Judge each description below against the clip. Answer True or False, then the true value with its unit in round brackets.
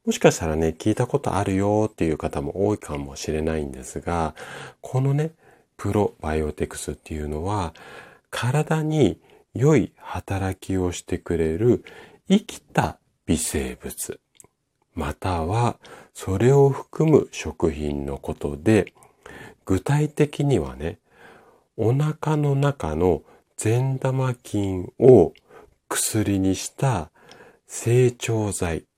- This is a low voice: True (100 Hz)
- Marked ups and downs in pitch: True (8.4 semitones)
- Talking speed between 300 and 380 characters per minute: False (215 characters per minute)